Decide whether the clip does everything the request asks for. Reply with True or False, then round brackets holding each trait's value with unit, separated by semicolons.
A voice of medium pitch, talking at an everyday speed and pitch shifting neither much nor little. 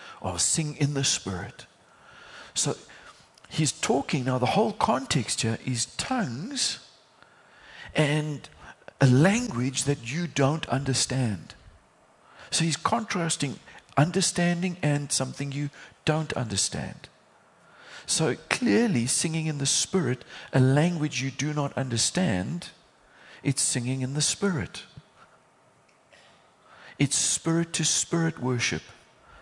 False (145 Hz; 110 wpm; 3.9 semitones)